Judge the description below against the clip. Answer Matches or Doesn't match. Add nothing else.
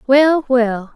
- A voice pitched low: Doesn't match